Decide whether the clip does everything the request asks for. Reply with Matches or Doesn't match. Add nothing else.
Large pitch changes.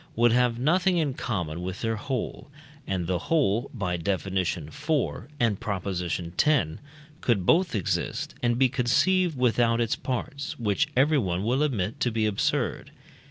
Matches